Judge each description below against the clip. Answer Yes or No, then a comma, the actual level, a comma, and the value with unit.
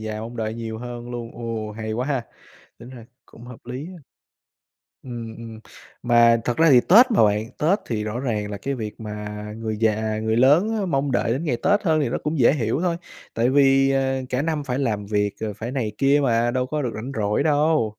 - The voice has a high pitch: No, low, 120 Hz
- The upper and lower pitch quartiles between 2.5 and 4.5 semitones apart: Yes, average, 3.9 semitones